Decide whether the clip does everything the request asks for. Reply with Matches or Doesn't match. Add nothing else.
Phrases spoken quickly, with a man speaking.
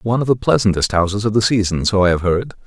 Matches